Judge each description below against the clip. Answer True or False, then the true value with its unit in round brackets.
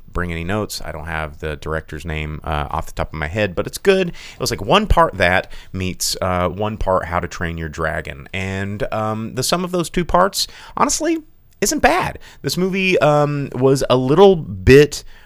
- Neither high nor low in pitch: False (100 Hz)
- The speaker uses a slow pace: False (205 wpm)